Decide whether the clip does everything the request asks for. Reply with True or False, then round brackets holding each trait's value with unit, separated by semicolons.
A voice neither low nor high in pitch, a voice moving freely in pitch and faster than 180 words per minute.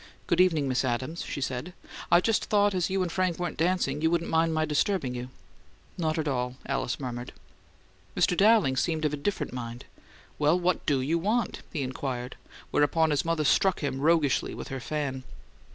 False (155 Hz; 4.9 semitones; 190 wpm)